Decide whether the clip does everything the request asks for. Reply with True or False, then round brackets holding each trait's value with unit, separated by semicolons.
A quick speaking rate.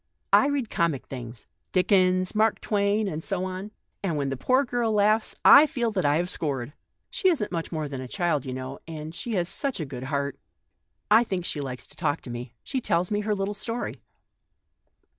True (215 wpm)